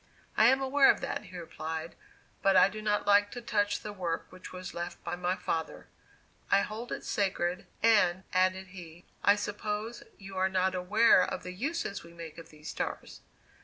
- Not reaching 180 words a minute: No, average, 190 wpm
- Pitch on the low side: No, high, 190 Hz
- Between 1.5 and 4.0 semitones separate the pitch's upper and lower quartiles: Yes, average, 2.9 semitones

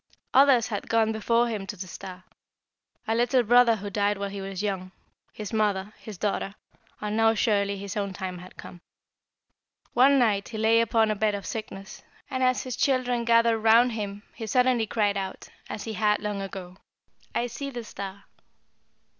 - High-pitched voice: Yes, high, 215 Hz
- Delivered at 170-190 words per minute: Yes, average, 180 wpm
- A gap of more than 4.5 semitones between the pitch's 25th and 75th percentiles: No, average, 2.7 semitones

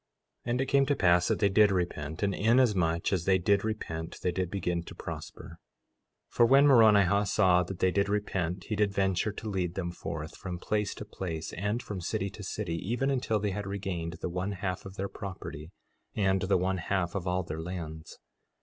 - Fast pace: Yes, fast, 210 wpm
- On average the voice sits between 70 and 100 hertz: Yes, very low, 95 Hz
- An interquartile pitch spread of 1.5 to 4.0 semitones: Yes, average, 2.9 semitones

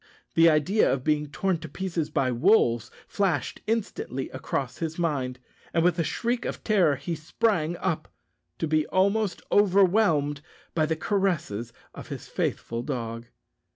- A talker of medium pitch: Yes, medium, 160 Hz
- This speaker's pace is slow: No, average, 150 wpm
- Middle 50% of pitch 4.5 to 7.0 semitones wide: Yes, average, 5.3 semitones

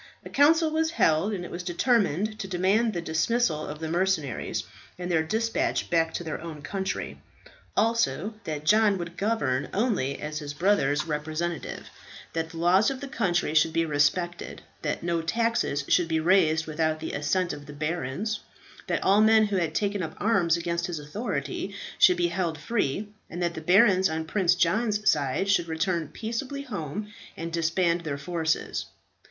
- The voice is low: No, medium, 175 Hz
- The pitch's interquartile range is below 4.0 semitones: No, average, 4.5 semitones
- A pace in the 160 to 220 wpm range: Yes, average, 175 wpm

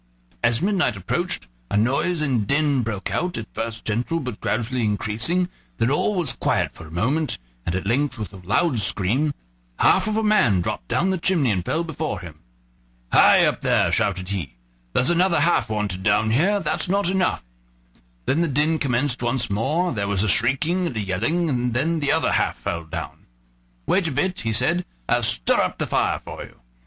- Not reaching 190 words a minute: No, average, 195 wpm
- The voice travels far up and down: Yes, wide, 7.8 semitones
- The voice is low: Yes, low, 125 Hz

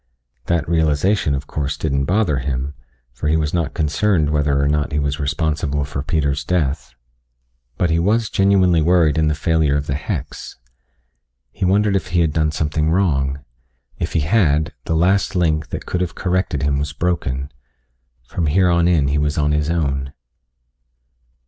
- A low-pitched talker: Yes, very low, 75 Hz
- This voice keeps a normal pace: Yes, average, 175 wpm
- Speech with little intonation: No, average, 3.3 semitones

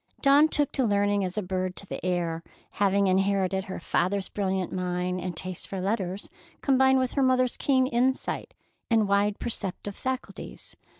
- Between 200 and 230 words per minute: No, average, 165 wpm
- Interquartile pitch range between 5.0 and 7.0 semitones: Yes, average, 5.3 semitones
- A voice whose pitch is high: Yes, high, 200 Hz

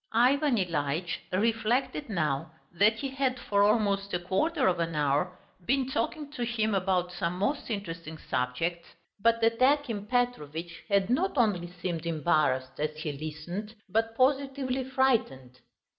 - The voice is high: Yes, high, 200 Hz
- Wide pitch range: Yes, wide, 6.8 semitones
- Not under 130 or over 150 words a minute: Yes, average, 145 wpm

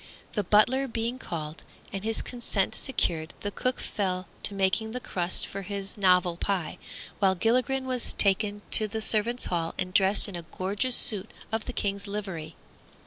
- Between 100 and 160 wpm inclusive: No, average, 170 wpm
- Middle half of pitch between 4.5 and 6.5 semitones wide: No, average, 3.2 semitones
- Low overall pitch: No, high, 200 Hz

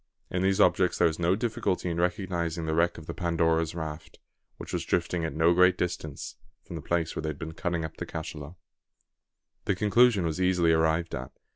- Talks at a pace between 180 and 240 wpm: Yes, average, 200 wpm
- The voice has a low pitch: Yes, very low, 85 Hz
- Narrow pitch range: Yes, narrow, 2.1 semitones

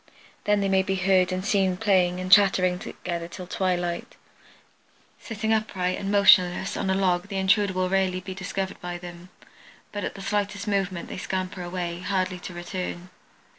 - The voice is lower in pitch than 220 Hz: Yes, medium, 185 Hz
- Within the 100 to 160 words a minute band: No, average, 170 wpm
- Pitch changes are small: Yes, narrow, 1.5 semitones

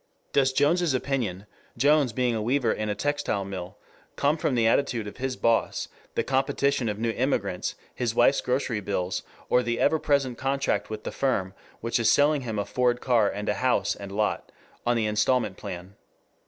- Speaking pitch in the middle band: No, low, 120 Hz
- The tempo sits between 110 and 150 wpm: No, average, 185 wpm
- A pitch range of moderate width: Yes, average, 4.2 semitones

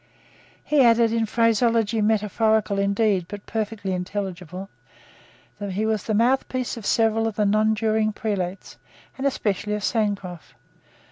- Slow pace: Yes, slow, 130 wpm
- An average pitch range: No, narrow, 2.1 semitones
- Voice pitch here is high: Yes, high, 215 Hz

